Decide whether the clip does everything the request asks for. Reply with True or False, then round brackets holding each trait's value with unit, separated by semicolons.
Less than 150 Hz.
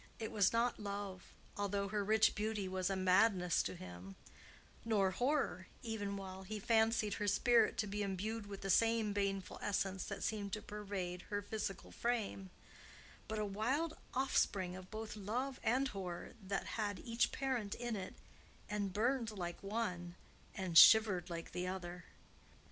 False (205 Hz)